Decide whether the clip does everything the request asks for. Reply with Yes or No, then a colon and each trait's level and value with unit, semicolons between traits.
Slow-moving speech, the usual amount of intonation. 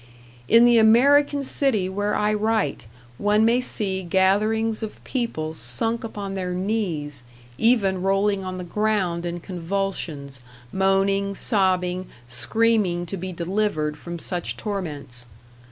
Yes: slow, 125 wpm; average, 3.8 semitones